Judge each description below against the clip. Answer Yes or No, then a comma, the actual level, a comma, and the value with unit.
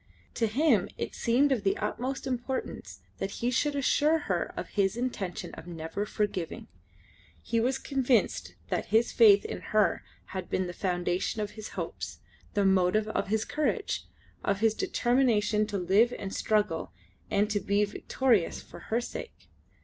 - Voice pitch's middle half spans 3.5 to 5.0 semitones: Yes, average, 4.1 semitones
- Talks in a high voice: Yes, high, 215 Hz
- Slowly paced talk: No, average, 160 wpm